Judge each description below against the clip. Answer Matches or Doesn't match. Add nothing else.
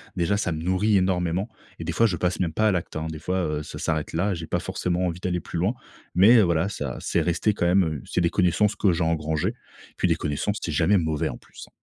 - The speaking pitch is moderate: Doesn't match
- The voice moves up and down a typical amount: Matches